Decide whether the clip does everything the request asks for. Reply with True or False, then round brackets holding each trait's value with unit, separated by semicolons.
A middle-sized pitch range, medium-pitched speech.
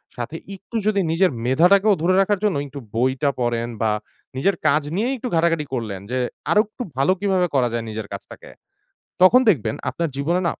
False (7.8 semitones; 165 Hz)